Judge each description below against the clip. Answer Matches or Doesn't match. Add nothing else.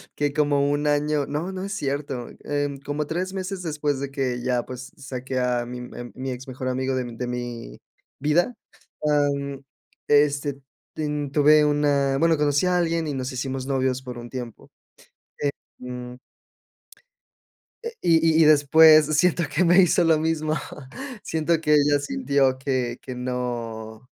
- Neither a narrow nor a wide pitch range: Matches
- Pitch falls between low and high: Matches